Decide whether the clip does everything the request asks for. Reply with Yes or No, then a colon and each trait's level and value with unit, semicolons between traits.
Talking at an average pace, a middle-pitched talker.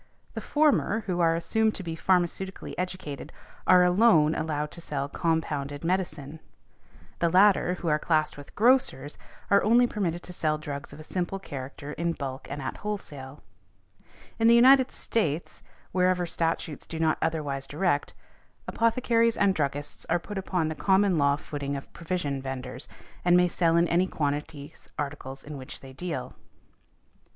Yes: average, 160 wpm; medium, 165 Hz